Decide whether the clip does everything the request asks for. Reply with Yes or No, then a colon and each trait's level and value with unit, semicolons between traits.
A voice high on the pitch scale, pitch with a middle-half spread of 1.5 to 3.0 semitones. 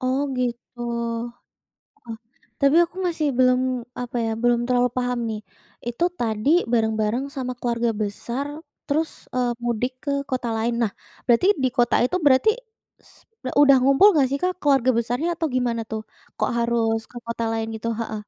Yes: high, 245 Hz; narrow, 2.4 semitones